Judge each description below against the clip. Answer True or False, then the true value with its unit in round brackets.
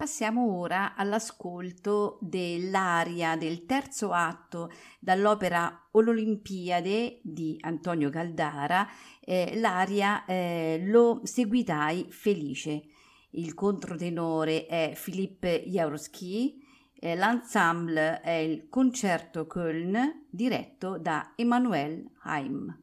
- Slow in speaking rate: True (85 wpm)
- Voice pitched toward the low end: False (185 Hz)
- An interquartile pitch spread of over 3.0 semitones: True (4.9 semitones)